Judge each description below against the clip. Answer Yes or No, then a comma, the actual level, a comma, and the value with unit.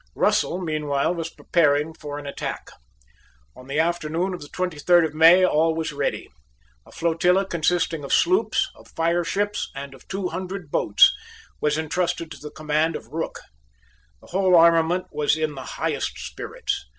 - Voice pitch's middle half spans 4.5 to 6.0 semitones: No, average, 3.0 semitones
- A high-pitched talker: No, medium, 160 Hz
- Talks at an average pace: Yes, average, 160 wpm